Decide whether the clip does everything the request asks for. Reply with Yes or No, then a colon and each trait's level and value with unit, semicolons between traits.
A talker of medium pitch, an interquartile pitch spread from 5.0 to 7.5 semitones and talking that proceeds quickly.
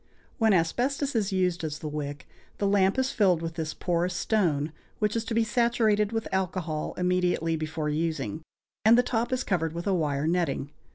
No: medium, 180 Hz; wide, 5.4 semitones; average, 185 wpm